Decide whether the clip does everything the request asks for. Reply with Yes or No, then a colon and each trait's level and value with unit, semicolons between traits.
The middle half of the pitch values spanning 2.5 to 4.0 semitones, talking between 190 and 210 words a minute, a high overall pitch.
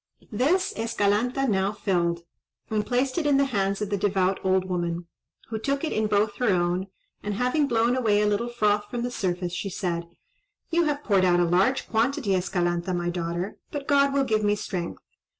No: average, 5.1 semitones; average, 195 wpm; high, 205 Hz